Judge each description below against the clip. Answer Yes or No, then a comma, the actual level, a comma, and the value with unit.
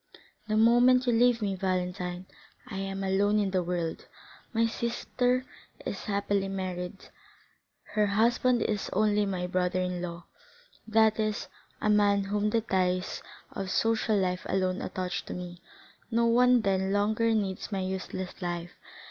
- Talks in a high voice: Yes, high, 200 Hz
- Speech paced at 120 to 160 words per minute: Yes, average, 150 wpm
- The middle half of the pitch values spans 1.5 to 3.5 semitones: Yes, average, 3.1 semitones